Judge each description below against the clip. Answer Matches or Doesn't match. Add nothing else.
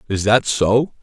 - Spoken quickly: Doesn't match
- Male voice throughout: Matches